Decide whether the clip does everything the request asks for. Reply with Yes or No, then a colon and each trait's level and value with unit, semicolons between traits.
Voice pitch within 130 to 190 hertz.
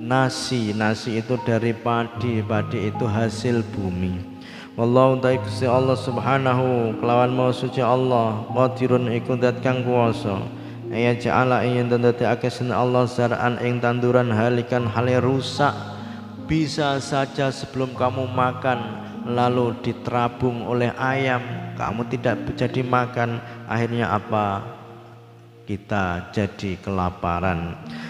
No: low, 120 Hz